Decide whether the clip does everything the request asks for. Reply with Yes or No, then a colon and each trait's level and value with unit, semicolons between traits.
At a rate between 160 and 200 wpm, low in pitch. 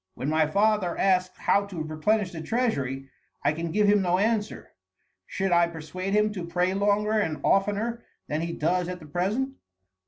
No: average, 180 wpm; medium, 185 Hz